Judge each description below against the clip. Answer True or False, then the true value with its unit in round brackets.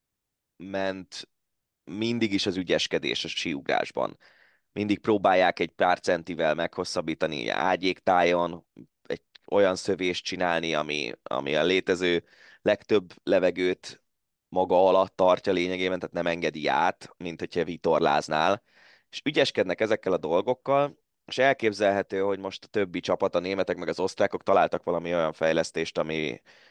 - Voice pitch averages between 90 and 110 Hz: True (95 Hz)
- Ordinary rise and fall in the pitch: False (2.3 semitones)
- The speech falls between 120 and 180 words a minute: True (130 wpm)